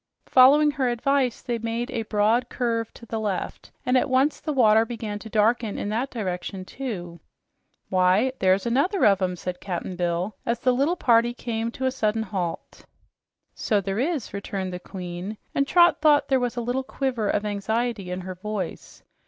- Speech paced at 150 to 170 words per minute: No, average, 180 wpm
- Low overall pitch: No, high, 225 Hz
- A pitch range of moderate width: Yes, average, 4.3 semitones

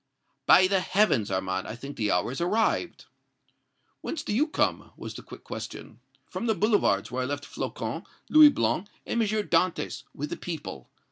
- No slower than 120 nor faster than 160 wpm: No, average, 175 wpm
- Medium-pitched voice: Yes, medium, 180 Hz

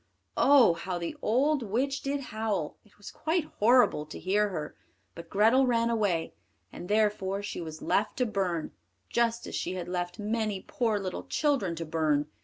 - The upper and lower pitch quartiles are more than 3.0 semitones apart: Yes, average, 4.8 semitones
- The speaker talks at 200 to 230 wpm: No, average, 175 wpm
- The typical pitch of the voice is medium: No, high, 205 Hz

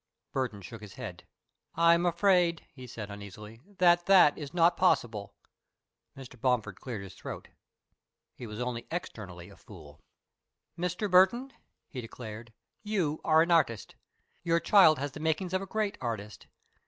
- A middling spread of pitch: No, wide, 7.9 semitones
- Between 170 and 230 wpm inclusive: No, average, 155 wpm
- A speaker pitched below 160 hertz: Yes, medium, 140 Hz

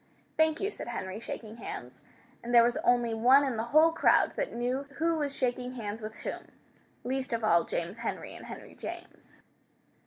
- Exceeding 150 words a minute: Yes, average, 185 wpm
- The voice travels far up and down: No, average, 3.5 semitones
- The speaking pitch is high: Yes, high, 240 Hz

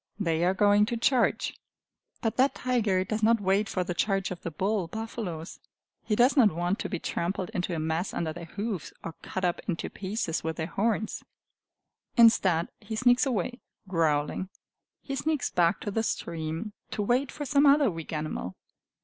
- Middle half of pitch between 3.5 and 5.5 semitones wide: Yes, average, 5.0 semitones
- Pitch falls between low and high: No, high, 195 Hz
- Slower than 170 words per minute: No, average, 180 wpm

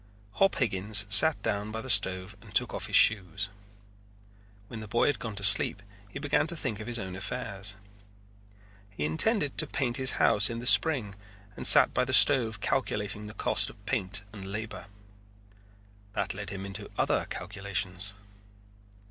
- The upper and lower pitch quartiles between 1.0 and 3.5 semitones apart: Yes, average, 3.2 semitones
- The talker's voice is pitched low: Yes, low, 105 Hz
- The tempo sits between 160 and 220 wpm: Yes, average, 170 wpm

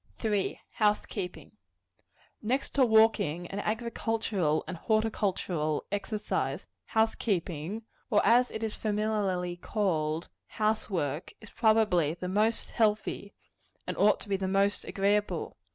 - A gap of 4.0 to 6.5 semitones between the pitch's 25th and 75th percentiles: No, average, 3.4 semitones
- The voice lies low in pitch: No, high, 205 Hz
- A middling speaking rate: No, slow, 125 wpm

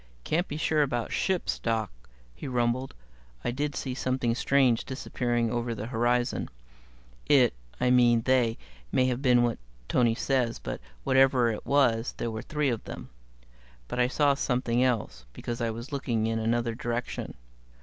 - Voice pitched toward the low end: Yes, low, 120 Hz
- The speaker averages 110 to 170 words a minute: Yes, average, 160 wpm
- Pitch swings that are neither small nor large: No, narrow, 2.1 semitones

